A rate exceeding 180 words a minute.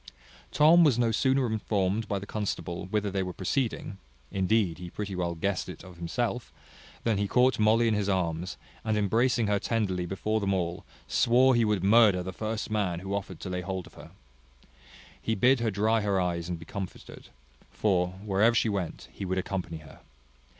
Yes: average, 190 wpm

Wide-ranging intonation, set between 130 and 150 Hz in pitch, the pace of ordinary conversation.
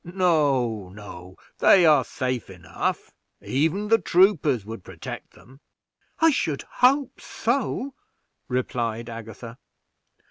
No: wide, 8.6 semitones; low, 135 Hz; slow, 105 wpm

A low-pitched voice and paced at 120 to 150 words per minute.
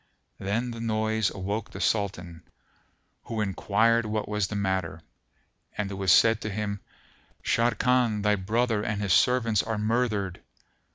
Yes: low, 105 Hz; average, 145 wpm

